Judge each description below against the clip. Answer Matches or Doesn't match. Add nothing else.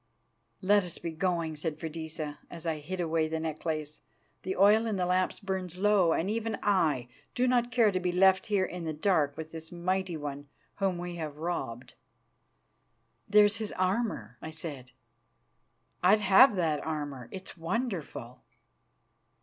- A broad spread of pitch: Doesn't match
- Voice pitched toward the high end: Doesn't match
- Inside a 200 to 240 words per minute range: Doesn't match